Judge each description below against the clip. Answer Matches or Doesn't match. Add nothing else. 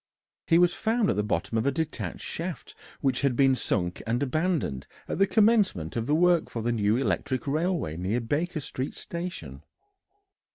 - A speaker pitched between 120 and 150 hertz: Matches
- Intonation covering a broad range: Matches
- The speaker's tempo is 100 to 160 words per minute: Doesn't match